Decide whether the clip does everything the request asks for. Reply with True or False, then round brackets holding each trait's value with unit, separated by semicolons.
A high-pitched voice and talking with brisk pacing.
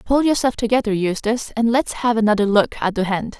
True (225 Hz; 210 wpm)